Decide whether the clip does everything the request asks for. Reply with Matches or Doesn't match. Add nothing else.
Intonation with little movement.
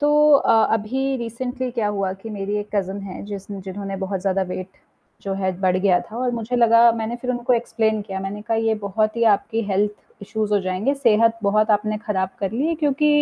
Doesn't match